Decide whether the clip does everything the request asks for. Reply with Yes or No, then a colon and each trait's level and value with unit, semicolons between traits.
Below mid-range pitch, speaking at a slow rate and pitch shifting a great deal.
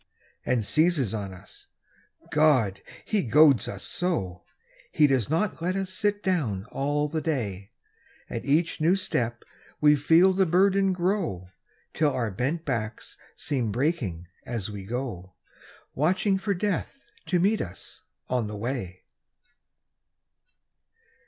No: medium, 145 Hz; slow, 130 wpm; wide, 8.5 semitones